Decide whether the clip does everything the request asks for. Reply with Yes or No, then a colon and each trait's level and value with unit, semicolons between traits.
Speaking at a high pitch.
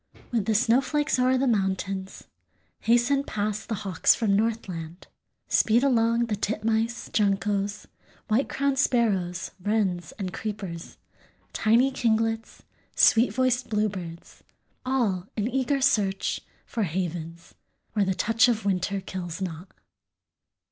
Yes: high, 215 Hz